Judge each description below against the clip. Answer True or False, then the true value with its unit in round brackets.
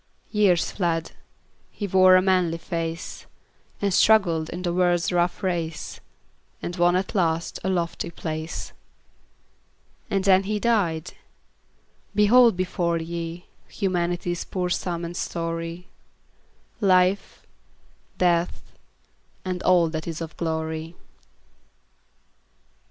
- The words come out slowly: True (105 wpm)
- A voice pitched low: False (175 Hz)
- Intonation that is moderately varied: False (1.9 semitones)